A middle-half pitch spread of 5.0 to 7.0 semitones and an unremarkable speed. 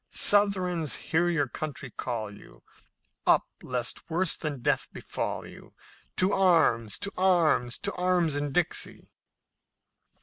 No: wide, 5.6 semitones; slow, 125 wpm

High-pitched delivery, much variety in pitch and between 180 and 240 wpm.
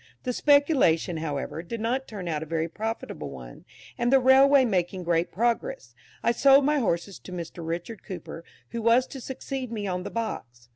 Yes: high, 215 Hz; wide, 7.5 semitones; average, 185 wpm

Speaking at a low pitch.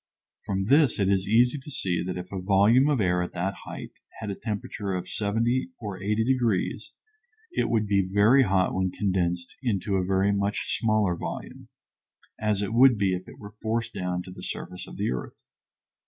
Yes: low, 100 Hz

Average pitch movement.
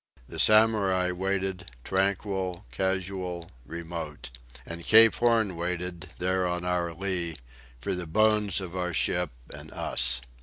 No: narrow, 2.0 semitones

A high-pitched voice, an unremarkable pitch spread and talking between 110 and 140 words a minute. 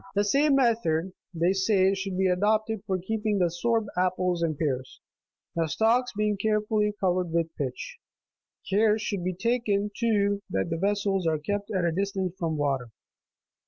No: high, 195 Hz; average, 3.7 semitones; average, 160 wpm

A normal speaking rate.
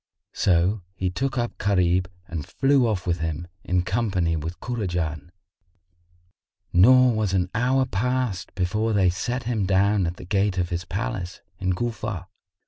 Yes: average, 150 wpm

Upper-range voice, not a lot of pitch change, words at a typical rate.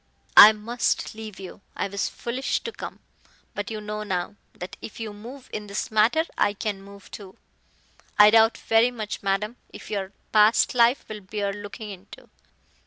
Yes: high, 210 Hz; narrow, 1.9 semitones; average, 175 wpm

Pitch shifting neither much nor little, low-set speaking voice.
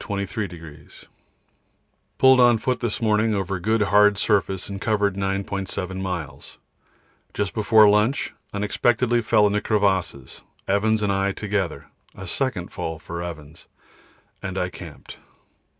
No: narrow, 2.3 semitones; low, 100 Hz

